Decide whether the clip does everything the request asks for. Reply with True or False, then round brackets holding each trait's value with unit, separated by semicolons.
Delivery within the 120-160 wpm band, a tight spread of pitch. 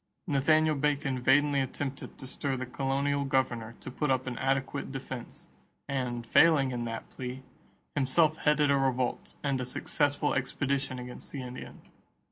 True (150 wpm; 1.9 semitones)